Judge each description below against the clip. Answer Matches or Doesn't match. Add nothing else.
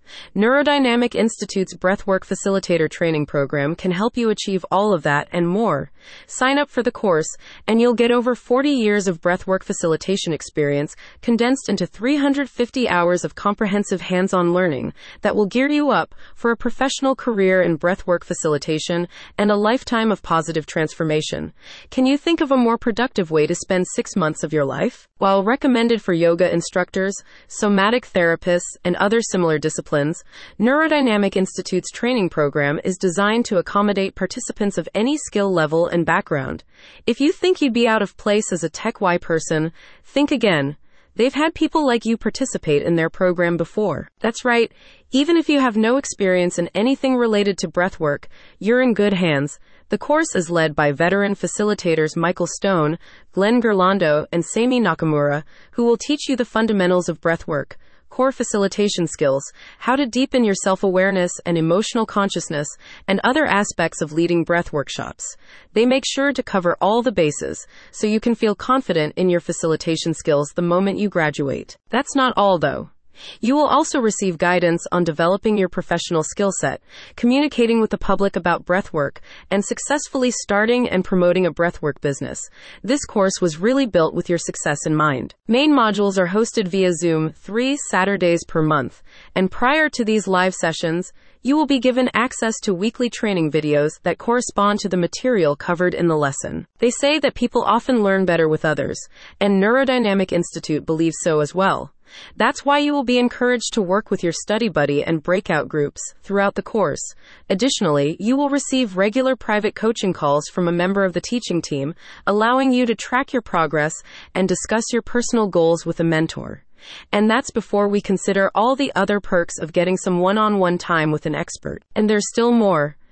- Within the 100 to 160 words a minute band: Doesn't match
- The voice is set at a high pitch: Matches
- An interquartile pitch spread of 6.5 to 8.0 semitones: Doesn't match